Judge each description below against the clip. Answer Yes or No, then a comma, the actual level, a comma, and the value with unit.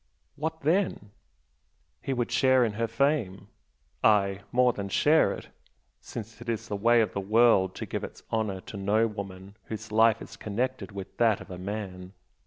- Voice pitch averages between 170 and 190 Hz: No, low, 110 Hz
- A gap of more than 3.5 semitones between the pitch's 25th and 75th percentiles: No, average, 3.2 semitones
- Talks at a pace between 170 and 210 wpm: Yes, average, 180 wpm